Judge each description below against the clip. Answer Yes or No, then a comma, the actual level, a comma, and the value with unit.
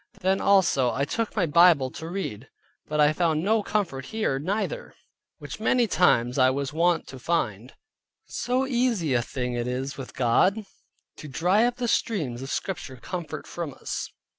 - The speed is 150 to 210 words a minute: Yes, average, 170 wpm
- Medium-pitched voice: Yes, medium, 160 Hz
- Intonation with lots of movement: Yes, wide, 7.1 semitones